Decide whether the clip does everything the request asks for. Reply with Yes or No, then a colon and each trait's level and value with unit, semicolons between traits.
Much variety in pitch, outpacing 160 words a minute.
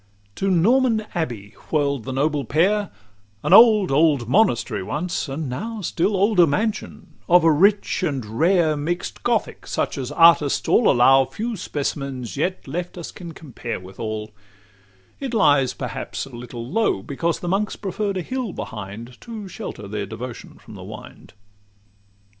No: wide, 7.4 semitones; average, 155 wpm